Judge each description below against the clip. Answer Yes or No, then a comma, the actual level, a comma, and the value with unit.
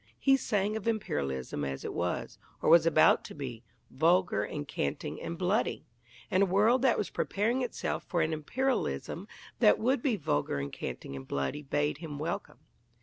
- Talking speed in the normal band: Yes, average, 175 wpm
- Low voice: No, medium, 165 Hz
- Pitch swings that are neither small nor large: No, wide, 8.9 semitones